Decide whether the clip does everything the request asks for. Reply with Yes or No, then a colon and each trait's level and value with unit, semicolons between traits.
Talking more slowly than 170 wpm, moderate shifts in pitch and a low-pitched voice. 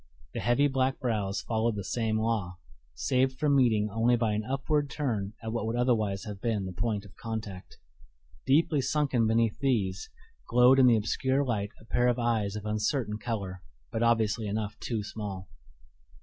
No: average, 175 wpm; average, 3.0 semitones; low, 115 Hz